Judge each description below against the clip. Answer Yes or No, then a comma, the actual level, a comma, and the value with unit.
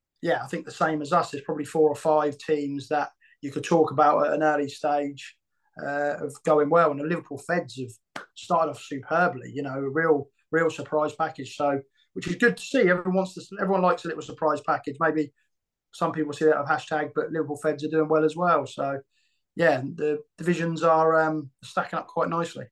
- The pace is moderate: No, fast, 215 wpm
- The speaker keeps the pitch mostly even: Yes, narrow, 2.2 semitones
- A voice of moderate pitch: Yes, medium, 155 Hz